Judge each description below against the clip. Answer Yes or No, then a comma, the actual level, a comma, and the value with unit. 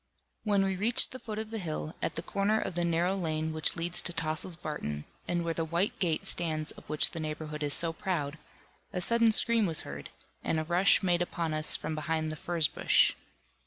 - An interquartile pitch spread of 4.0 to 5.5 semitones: No, average, 3.4 semitones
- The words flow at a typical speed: No, fast, 215 wpm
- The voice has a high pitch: No, medium, 170 Hz